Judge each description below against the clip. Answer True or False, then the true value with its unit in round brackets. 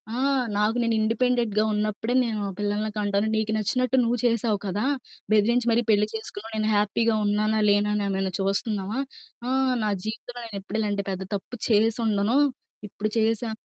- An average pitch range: False (2.0 semitones)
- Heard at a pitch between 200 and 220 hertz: True (215 Hz)